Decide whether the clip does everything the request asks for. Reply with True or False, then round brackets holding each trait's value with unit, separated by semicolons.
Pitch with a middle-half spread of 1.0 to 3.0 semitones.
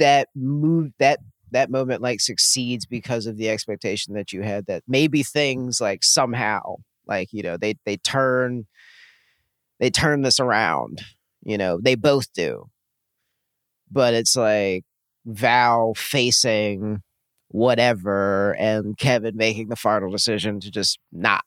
False (3.6 semitones)